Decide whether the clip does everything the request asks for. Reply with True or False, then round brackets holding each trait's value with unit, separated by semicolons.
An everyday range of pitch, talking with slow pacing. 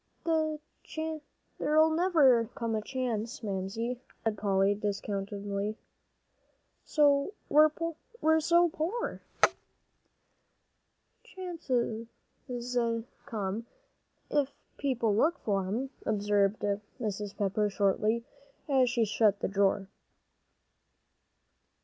False (6.6 semitones; 75 wpm)